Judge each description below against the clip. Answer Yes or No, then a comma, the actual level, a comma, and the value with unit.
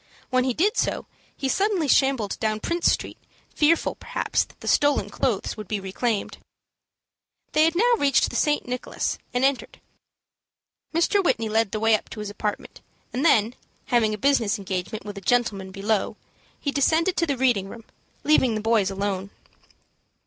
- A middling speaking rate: Yes, average, 170 wpm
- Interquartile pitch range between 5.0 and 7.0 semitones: Yes, wide, 5.5 semitones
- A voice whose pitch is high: Yes, high, 235 Hz